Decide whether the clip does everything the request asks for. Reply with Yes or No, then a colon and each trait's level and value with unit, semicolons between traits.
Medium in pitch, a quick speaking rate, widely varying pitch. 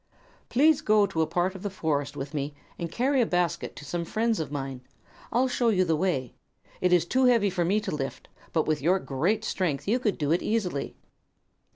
Yes: medium, 180 Hz; fast, 215 wpm; wide, 5.9 semitones